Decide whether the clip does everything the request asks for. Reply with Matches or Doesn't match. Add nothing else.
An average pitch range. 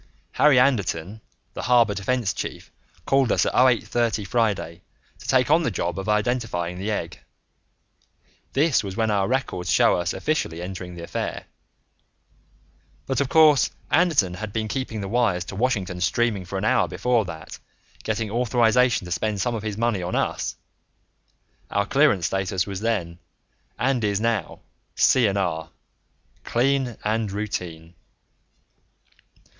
Matches